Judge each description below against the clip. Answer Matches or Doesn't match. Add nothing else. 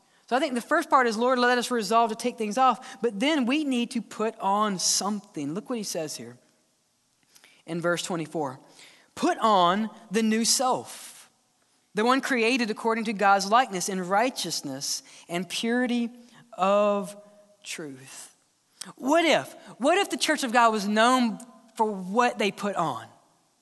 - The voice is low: Doesn't match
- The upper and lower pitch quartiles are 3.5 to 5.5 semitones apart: Matches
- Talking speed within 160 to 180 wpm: Matches